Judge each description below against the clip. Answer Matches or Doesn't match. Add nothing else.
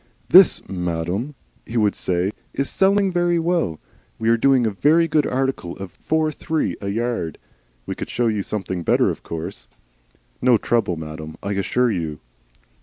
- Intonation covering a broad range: Matches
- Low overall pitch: Matches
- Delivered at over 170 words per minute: Doesn't match